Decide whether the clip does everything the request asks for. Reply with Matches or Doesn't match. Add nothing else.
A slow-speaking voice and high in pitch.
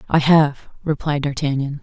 Doesn't match